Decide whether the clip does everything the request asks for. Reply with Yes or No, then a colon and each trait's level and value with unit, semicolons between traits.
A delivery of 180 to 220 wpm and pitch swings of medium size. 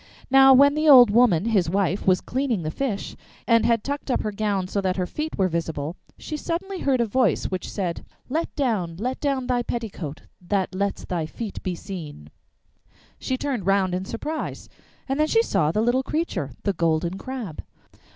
No: average, 190 wpm; wide, 6.4 semitones